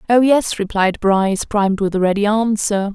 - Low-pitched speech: No, high, 205 Hz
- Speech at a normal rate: Yes, average, 185 wpm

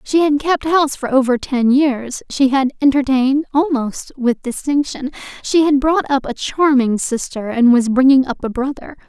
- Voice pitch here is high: Yes, very high, 270 Hz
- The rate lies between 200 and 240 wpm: No, average, 180 wpm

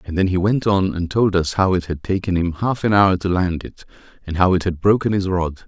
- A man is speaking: Yes, male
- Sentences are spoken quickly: Yes, fast, 275 wpm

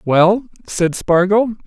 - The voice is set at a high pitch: Yes, high, 195 Hz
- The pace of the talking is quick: No, slow, 110 wpm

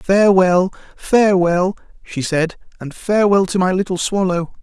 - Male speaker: Yes, male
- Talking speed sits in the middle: No, slow, 130 wpm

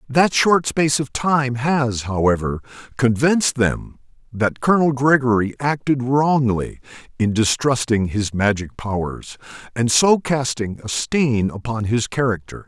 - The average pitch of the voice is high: No, low, 125 Hz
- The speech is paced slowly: Yes, slow, 130 wpm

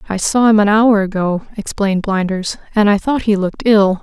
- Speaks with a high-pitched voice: Yes, high, 205 Hz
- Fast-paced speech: Yes, fast, 210 wpm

